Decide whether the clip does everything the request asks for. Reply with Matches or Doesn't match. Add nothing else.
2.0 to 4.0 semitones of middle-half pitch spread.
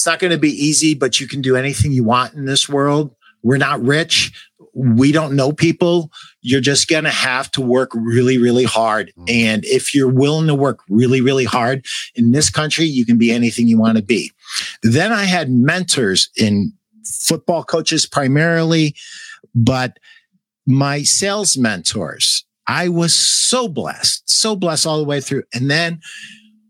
Doesn't match